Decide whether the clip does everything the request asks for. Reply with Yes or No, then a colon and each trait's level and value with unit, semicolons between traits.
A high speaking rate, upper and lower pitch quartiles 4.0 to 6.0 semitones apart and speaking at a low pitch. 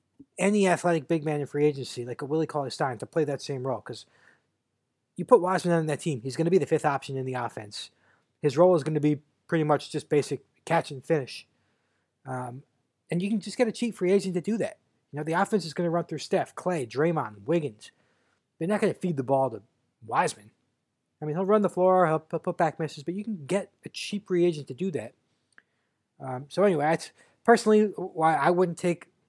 No: fast, 230 wpm; average, 4.6 semitones; medium, 160 Hz